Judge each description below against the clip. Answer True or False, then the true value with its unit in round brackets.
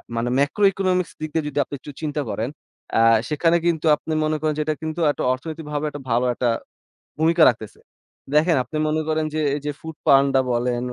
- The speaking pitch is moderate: True (155 Hz)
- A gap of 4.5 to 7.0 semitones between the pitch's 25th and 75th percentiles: False (2.7 semitones)